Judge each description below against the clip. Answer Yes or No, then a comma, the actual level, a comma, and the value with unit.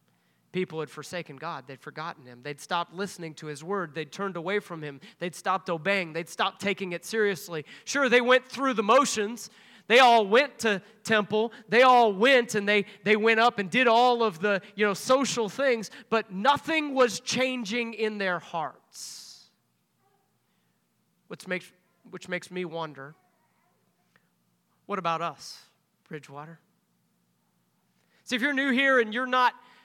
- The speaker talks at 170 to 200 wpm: No, average, 160 wpm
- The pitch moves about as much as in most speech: No, wide, 5.8 semitones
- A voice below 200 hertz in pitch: No, high, 205 Hz